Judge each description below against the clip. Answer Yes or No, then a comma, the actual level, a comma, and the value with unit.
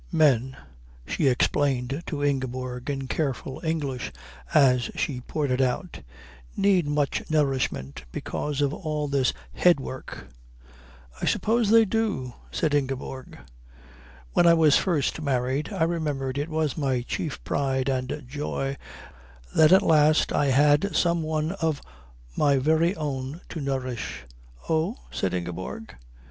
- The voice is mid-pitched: Yes, medium, 145 Hz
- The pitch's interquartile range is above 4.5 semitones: No, average, 3.3 semitones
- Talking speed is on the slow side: Yes, slow, 130 wpm